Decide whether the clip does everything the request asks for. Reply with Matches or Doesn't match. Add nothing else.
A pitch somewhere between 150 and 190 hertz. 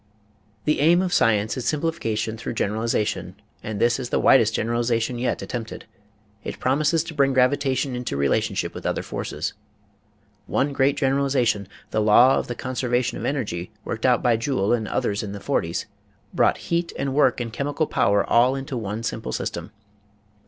Doesn't match